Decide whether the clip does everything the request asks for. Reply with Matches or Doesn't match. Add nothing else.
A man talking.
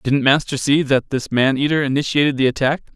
Matches